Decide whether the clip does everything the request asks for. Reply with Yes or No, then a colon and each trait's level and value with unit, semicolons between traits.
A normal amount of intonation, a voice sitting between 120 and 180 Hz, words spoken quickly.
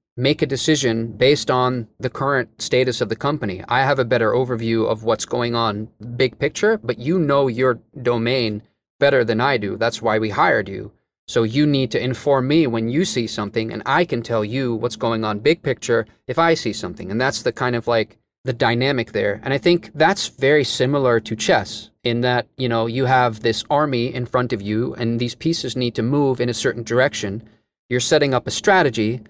Yes: average, 3.0 semitones; low, 125 Hz; fast, 215 wpm